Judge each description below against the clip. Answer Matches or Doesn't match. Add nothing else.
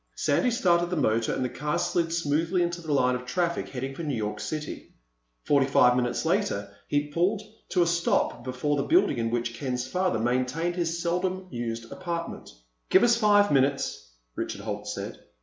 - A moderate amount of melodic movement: Doesn't match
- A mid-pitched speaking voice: Matches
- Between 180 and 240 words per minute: Matches